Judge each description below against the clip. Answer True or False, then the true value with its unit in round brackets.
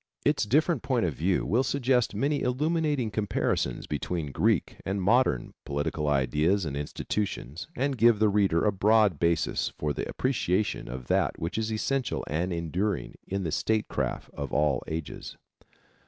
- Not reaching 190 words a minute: True (155 wpm)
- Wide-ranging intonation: True (7.3 semitones)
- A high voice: False (100 Hz)